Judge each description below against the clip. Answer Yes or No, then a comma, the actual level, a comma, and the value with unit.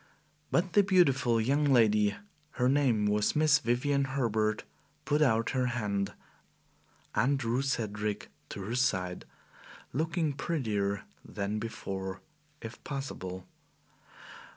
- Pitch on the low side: Yes, low, 120 Hz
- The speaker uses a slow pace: Yes, slow, 110 wpm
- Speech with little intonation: No, average, 4.8 semitones